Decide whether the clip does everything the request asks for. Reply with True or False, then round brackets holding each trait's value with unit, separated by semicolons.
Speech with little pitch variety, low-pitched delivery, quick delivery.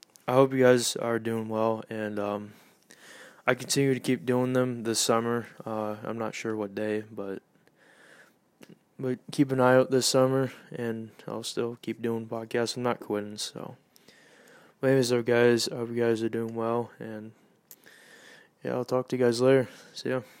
False (2.3 semitones; 115 Hz; 180 wpm)